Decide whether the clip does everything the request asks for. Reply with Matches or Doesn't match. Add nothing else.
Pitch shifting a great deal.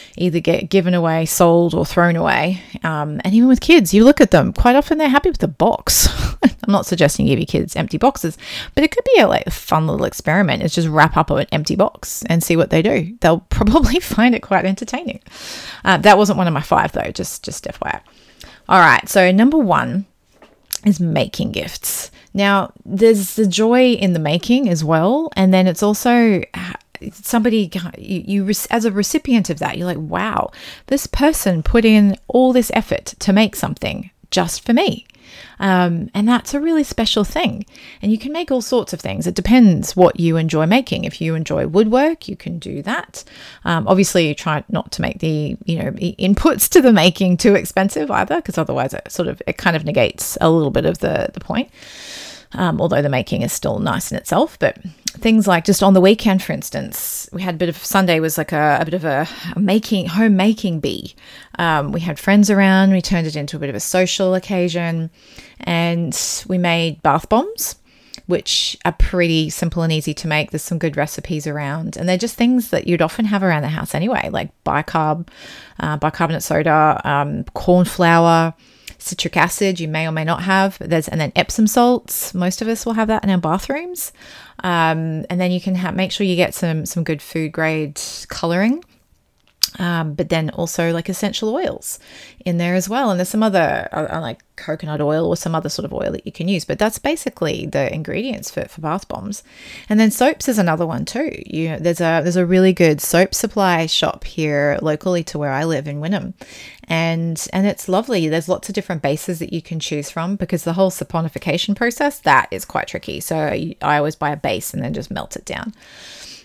Doesn't match